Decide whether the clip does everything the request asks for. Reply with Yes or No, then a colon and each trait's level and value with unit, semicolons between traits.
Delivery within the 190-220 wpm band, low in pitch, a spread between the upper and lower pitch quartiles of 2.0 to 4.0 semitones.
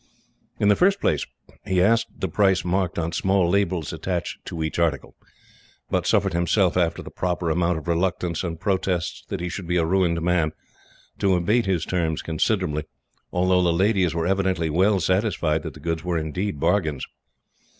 No: average, 175 wpm; very low, 90 Hz; narrow, 2.4 semitones